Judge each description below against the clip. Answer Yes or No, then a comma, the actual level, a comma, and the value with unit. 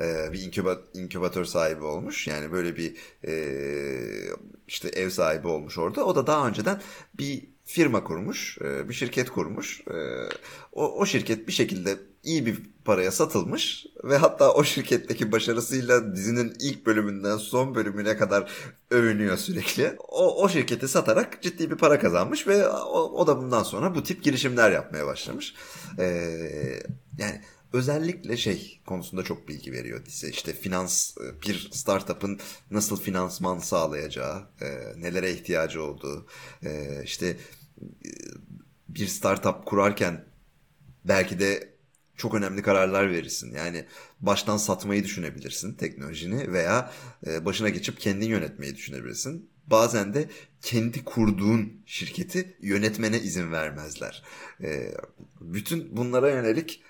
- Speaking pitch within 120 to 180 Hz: No, low, 105 Hz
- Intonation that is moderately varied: No, wide, 7.2 semitones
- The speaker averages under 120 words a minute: No, average, 125 wpm